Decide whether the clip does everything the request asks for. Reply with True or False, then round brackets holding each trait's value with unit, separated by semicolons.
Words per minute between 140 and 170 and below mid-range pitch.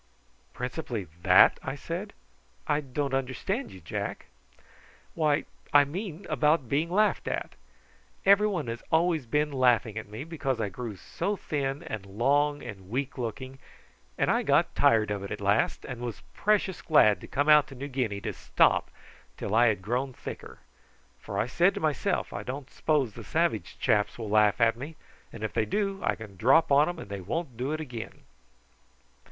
False (180 wpm; 130 Hz)